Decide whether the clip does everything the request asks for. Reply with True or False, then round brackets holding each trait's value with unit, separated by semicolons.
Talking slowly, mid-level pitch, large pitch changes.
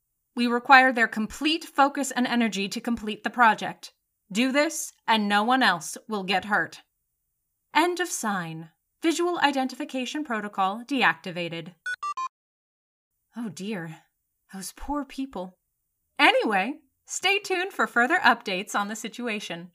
False (125 wpm; 235 Hz; 5.7 semitones)